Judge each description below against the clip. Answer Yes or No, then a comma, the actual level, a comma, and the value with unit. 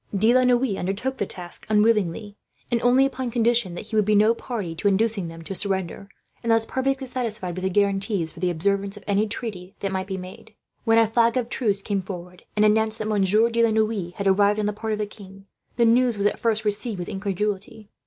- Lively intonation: No, average, 2.8 semitones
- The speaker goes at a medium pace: No, fast, 225 wpm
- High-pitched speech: Yes, high, 210 Hz